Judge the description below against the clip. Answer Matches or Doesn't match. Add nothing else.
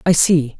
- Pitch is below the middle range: Doesn't match